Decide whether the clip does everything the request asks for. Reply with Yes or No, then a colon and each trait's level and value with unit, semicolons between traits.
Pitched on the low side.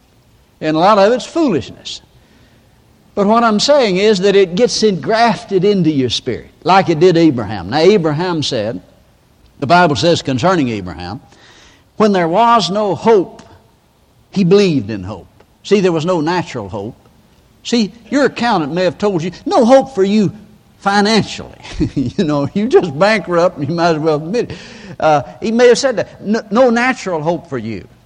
No: medium, 185 Hz